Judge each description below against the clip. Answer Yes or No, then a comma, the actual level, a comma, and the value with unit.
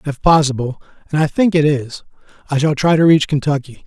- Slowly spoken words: No, average, 200 wpm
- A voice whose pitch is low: No, medium, 150 Hz